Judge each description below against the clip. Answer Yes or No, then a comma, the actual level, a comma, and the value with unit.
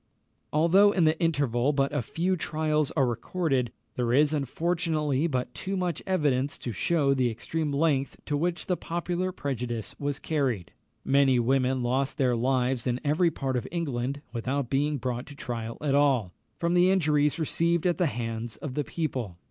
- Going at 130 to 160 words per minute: No, average, 170 wpm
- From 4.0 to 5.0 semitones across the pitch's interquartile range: Yes, average, 4.4 semitones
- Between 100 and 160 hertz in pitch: Yes, medium, 140 Hz